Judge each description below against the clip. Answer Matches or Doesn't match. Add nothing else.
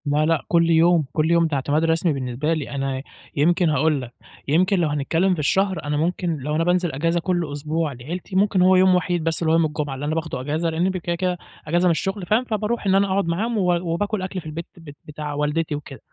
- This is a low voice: Doesn't match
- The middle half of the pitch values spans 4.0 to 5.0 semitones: Doesn't match